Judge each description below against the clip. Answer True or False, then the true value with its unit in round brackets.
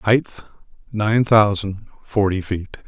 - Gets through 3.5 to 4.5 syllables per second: True (4.0 syllables/s)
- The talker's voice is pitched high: False (105 Hz)